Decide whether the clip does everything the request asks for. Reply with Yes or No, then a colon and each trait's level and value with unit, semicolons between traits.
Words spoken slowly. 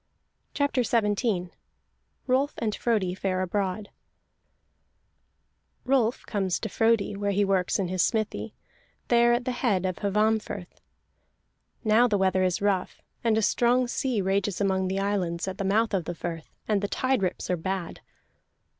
No: average, 155 wpm